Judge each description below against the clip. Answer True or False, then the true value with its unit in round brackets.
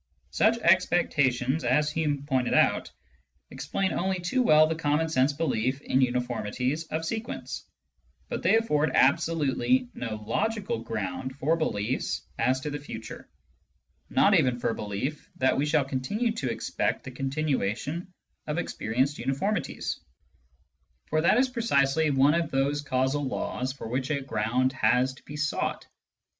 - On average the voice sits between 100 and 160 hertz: True (140 Hz)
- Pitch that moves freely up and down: False (4.0 semitones)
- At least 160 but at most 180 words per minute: False (150 wpm)